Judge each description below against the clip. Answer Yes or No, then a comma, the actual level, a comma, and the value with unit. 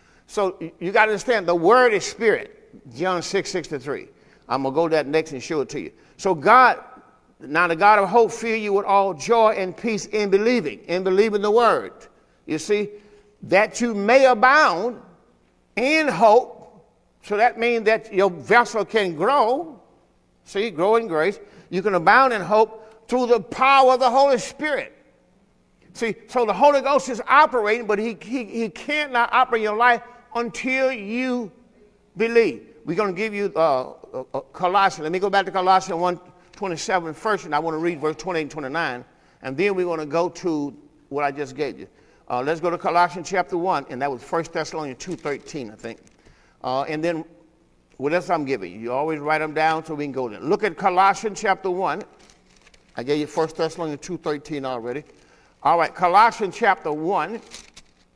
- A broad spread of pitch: Yes, wide, 5.9 semitones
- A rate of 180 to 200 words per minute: Yes, average, 190 wpm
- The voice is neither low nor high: No, high, 195 Hz